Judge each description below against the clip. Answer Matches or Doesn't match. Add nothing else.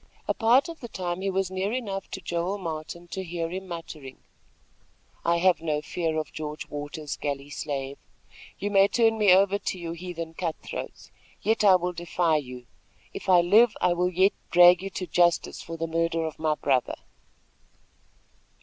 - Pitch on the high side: Doesn't match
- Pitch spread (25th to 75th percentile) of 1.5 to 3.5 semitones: Matches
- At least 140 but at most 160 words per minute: Doesn't match